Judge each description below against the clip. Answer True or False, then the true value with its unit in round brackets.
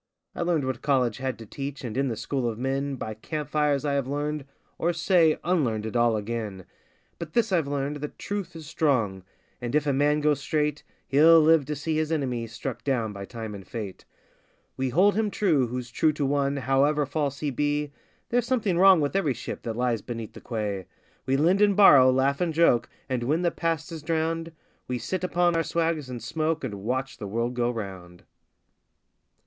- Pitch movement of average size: True (5.0 semitones)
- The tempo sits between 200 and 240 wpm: True (205 wpm)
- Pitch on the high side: False (140 Hz)